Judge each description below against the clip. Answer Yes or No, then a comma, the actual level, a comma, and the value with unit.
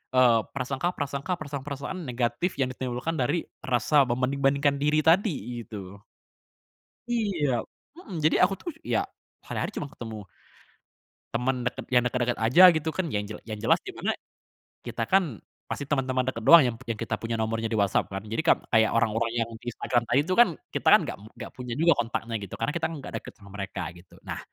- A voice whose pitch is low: Yes, low, 130 Hz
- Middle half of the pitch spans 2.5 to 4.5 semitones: No, average, 4.9 semitones